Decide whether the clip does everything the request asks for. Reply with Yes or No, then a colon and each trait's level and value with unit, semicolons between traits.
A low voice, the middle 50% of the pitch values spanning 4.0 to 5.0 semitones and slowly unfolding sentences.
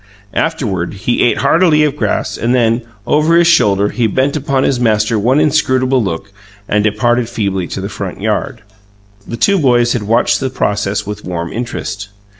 No: low, 120 Hz; average, 4.5 semitones; average, 175 wpm